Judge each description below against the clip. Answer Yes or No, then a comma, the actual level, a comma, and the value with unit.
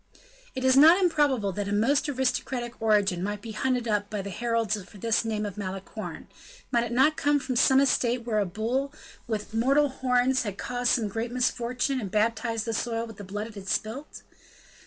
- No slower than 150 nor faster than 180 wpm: No, average, 200 wpm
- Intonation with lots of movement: No, average, 3.7 semitones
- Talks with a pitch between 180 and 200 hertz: No, high, 230 Hz